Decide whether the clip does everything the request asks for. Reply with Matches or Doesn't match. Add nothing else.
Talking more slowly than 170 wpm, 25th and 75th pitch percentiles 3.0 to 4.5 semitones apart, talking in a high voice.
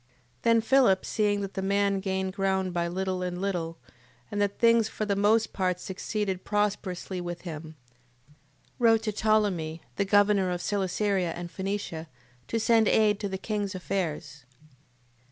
Doesn't match